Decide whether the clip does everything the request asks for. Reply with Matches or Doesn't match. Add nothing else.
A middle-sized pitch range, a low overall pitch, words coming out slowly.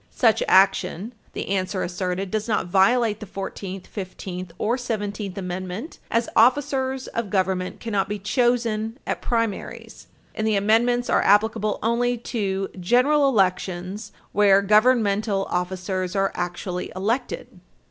Doesn't match